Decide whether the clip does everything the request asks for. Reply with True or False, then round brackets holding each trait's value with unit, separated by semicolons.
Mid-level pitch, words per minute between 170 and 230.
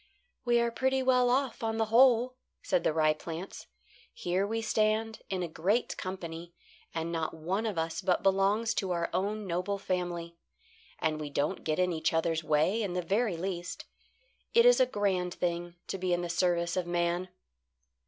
True (180 Hz; 185 wpm)